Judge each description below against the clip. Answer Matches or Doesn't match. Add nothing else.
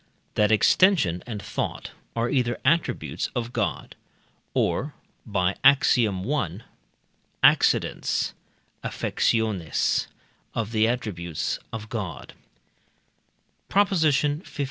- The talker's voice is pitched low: Matches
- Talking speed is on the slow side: Matches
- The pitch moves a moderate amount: Doesn't match